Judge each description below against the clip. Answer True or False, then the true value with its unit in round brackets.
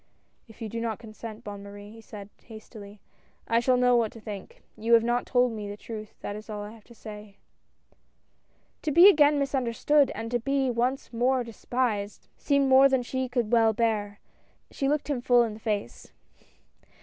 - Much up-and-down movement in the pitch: False (3.0 semitones)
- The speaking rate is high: False (195 wpm)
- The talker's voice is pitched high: True (230 Hz)